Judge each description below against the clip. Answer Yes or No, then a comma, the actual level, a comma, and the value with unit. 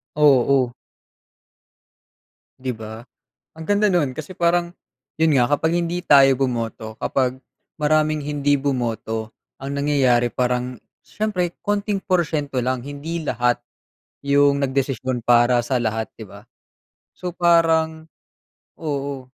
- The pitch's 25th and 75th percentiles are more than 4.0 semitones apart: Yes, average, 4.4 semitones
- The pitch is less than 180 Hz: Yes, medium, 140 Hz